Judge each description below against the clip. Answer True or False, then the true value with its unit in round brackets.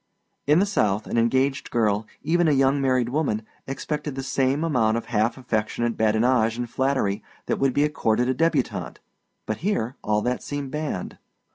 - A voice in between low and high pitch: False (130 Hz)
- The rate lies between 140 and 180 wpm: True (170 wpm)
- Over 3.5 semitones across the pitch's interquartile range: True (4.2 semitones)